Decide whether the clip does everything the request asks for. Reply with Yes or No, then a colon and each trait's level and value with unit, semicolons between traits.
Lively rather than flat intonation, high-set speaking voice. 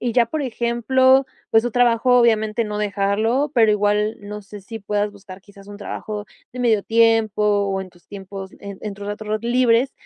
No: narrow, 2.6 semitones; high, 215 Hz